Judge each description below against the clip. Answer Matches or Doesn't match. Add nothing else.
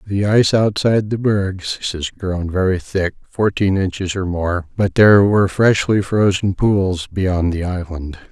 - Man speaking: Matches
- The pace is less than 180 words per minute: Matches